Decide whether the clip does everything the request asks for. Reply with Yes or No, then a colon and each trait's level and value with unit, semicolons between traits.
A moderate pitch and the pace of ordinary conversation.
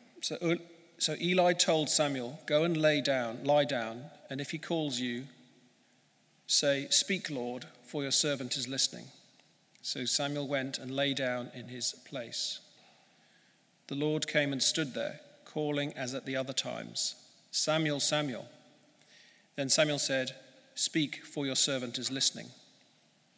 Yes: medium, 145 Hz; average, 145 wpm